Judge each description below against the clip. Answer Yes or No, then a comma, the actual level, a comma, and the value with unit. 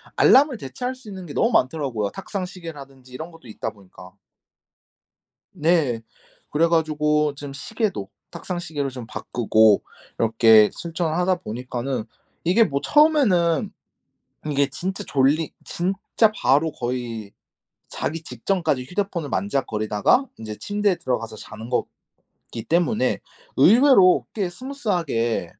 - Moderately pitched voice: Yes, medium, 155 Hz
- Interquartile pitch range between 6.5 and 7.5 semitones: Yes, wide, 6.9 semitones